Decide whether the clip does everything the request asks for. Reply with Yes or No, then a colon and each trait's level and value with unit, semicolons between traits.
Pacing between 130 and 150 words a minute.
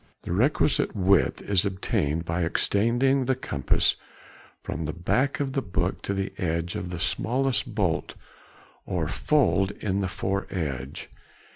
Yes: average, 140 wpm